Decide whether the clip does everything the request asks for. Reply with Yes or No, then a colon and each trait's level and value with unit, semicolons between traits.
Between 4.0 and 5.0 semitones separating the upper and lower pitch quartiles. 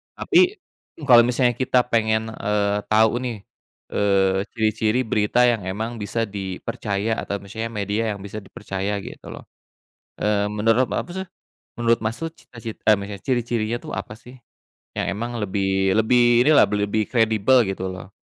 No: average, 2.8 semitones